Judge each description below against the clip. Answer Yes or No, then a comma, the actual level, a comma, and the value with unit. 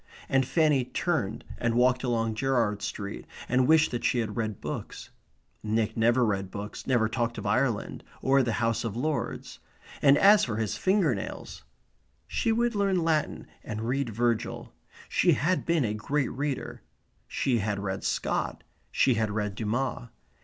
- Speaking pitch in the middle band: No, low, 120 Hz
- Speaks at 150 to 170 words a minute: Yes, average, 160 wpm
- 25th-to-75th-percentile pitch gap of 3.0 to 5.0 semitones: Yes, average, 4.1 semitones